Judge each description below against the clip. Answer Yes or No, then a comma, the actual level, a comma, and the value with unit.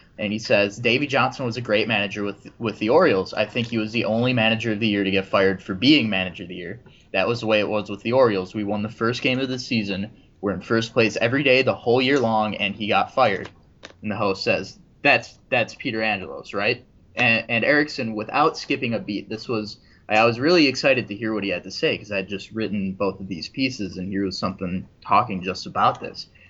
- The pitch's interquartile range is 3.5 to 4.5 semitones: No, average, 2.7 semitones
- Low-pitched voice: Yes, low, 110 Hz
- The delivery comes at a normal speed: No, fast, 245 wpm